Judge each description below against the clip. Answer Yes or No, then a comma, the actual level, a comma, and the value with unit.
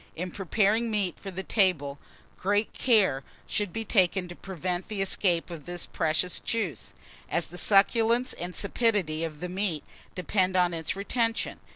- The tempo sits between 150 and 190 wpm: Yes, average, 160 wpm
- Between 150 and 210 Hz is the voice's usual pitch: Yes, medium, 185 Hz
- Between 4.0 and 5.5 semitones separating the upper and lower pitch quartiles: No, average, 3.2 semitones